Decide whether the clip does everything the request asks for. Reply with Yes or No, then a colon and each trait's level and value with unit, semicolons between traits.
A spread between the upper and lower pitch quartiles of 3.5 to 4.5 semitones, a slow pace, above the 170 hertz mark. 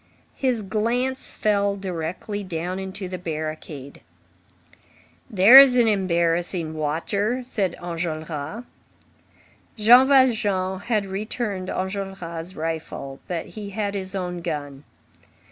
Yes: average, 4.1 semitones; slow, 100 wpm; high, 190 Hz